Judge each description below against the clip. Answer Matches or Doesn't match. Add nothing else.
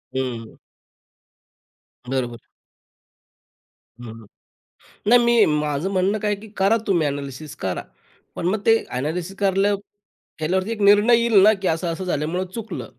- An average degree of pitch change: Doesn't match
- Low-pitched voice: Doesn't match